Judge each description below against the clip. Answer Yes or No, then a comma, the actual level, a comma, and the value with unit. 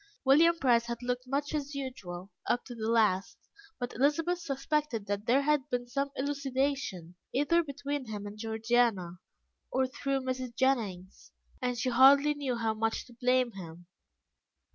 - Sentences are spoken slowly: No, average, 155 wpm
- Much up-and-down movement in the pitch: No, average, 3.9 semitones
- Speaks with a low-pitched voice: No, very high, 250 Hz